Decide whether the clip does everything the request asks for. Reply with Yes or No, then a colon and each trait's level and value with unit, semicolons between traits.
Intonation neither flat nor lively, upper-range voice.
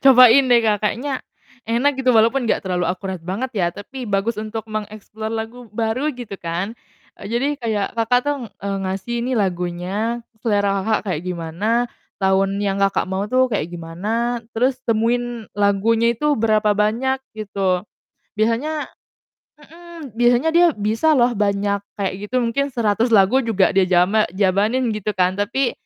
Yes: average, 3.6 semitones; high, 220 Hz